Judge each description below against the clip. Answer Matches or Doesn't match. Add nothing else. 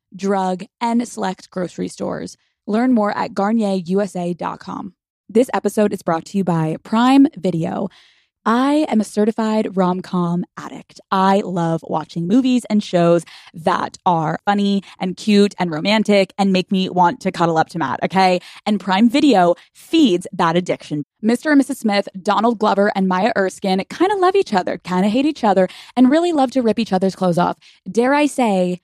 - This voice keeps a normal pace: Matches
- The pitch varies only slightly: Doesn't match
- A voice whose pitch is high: Matches